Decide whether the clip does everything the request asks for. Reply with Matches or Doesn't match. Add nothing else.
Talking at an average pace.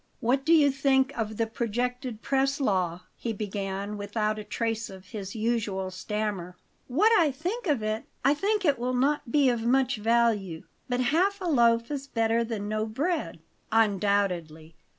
Matches